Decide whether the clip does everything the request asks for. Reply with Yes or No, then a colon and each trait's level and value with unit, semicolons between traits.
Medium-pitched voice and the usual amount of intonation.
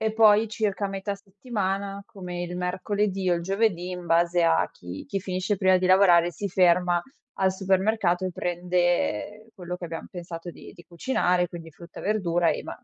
No: medium, 180 Hz; narrow, 2.3 semitones